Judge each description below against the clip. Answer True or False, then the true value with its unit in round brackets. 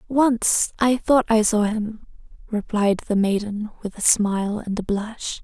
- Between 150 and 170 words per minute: True (165 wpm)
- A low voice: False (215 Hz)